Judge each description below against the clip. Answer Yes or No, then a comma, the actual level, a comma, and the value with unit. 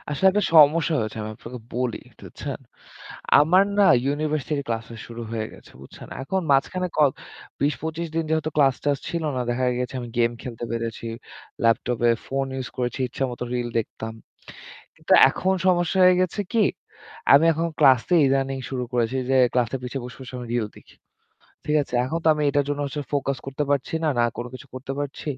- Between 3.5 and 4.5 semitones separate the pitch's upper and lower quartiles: Yes, average, 4.1 semitones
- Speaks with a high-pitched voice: No, low, 135 Hz